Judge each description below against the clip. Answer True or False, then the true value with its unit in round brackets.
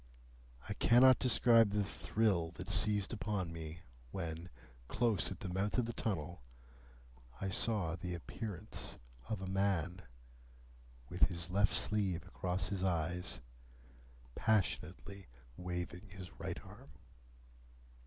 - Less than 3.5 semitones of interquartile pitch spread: True (3.1 semitones)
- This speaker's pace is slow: True (120 wpm)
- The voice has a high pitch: False (95 Hz)